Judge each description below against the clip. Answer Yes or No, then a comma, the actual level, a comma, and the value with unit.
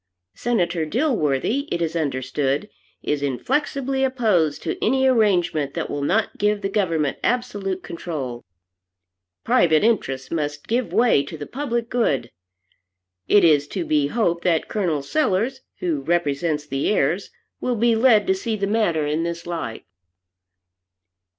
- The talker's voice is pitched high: No, medium, 175 Hz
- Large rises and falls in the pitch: Yes, wide, 7.2 semitones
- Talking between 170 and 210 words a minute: No, average, 140 wpm